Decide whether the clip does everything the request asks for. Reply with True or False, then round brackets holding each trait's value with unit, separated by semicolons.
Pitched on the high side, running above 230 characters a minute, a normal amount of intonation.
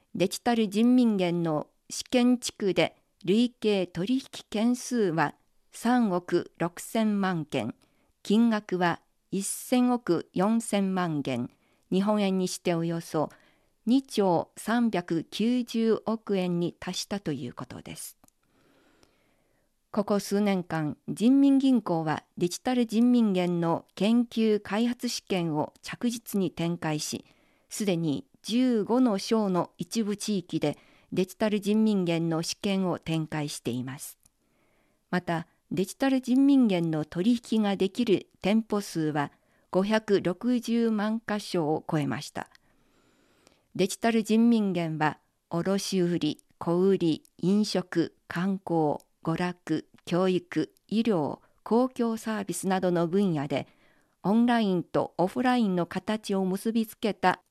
False (195 Hz; 215 characters per minute; 4.9 semitones)